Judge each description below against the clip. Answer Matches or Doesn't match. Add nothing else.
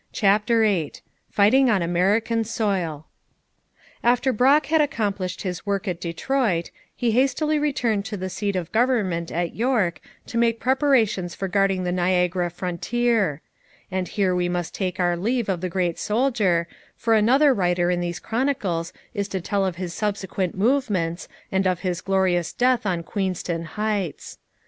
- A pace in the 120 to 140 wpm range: Doesn't match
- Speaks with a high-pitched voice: Matches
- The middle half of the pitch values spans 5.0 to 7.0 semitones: Doesn't match